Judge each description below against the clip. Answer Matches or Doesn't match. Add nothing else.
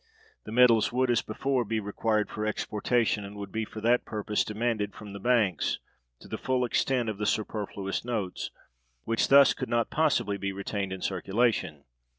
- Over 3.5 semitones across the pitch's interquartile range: Doesn't match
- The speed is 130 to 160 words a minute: Doesn't match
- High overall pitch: Doesn't match